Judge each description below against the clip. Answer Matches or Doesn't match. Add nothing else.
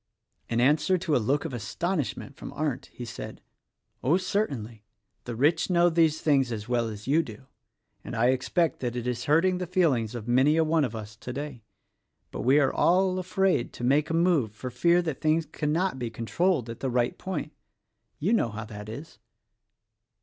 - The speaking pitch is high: Doesn't match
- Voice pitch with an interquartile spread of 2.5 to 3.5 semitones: Doesn't match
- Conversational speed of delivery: Matches